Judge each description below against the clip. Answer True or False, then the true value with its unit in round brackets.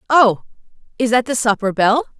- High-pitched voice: True (240 Hz)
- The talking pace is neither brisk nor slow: True (165 wpm)